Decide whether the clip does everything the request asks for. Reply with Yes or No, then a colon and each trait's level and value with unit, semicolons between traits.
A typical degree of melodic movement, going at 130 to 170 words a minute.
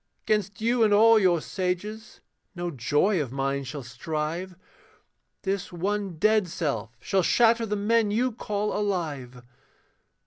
No: wide, 5.7 semitones; slow, 135 wpm